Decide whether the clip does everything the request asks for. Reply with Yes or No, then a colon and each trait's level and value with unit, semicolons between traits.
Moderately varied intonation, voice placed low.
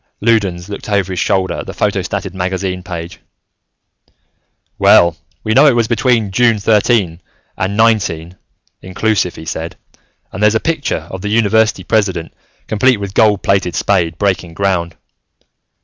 Yes: average, 3.5 semitones; low, 100 Hz